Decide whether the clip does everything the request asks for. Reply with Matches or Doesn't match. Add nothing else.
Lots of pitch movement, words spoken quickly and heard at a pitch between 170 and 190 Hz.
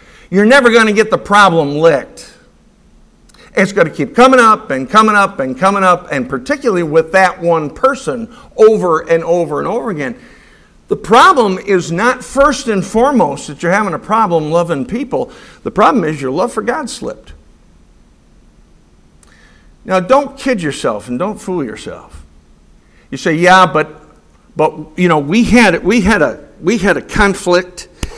Doesn't match